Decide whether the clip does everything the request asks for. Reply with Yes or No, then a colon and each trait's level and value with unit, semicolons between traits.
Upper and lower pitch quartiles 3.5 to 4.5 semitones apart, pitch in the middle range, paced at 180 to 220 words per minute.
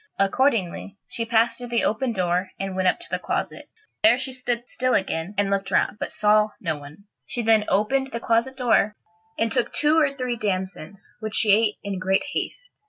No: average, 4.0 semitones; high, 215 Hz; average, 200 wpm